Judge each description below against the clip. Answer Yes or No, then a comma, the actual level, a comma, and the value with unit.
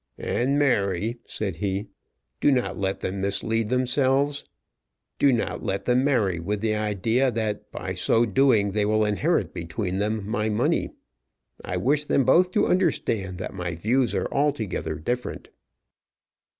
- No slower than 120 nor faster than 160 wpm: Yes, average, 150 wpm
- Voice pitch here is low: Yes, low, 110 Hz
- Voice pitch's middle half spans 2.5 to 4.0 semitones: No, average, 4.6 semitones